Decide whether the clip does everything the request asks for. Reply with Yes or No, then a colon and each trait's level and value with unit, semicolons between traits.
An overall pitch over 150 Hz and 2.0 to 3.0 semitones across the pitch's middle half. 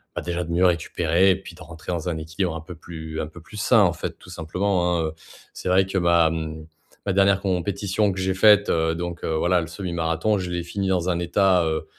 No: very low, 85 Hz; narrow, 2.5 semitones